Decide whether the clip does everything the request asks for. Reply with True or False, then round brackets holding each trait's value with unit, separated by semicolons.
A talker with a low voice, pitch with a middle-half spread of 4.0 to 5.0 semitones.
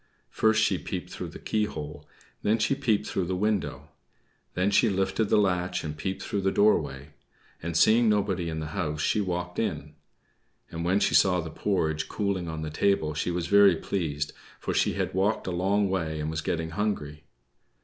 True (90 Hz; 4.3 semitones)